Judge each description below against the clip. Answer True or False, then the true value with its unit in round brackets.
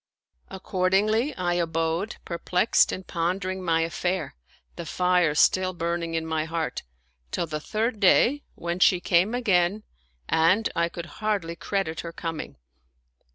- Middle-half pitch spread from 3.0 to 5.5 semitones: False (2.6 semitones)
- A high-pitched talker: False (175 Hz)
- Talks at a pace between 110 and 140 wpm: True (135 wpm)